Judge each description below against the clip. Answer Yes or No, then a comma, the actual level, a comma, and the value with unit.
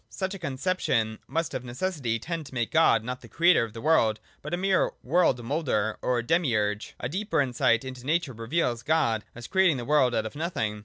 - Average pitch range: No, wide, 6.3 semitones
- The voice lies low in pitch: Yes, low, 130 Hz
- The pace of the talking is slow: No, fast, 205 wpm